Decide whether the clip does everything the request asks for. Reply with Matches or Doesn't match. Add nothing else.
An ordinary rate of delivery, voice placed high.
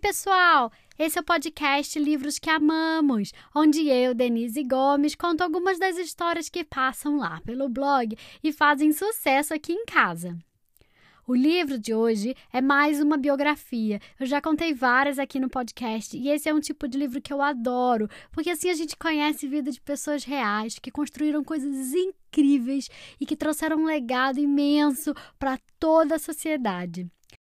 Matches